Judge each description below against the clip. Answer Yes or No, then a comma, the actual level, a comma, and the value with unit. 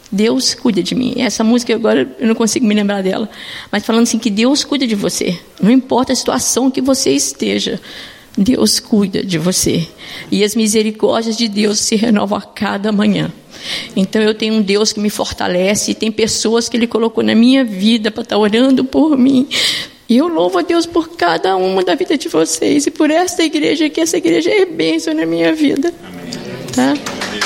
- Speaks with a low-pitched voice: No, high, 230 Hz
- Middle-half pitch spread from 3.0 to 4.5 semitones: Yes, average, 4.0 semitones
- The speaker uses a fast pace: Yes, fast, 195 wpm